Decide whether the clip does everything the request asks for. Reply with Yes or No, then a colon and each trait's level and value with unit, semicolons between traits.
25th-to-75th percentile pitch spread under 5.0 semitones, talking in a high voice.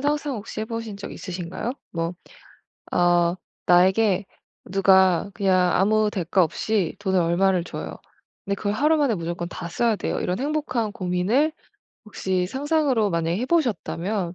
Yes: average, 4.3 semitones; high, 195 Hz